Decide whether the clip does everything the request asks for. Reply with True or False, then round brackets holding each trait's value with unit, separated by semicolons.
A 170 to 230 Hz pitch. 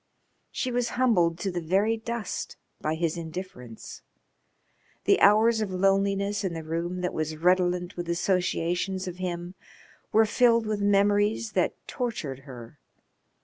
True (185 Hz)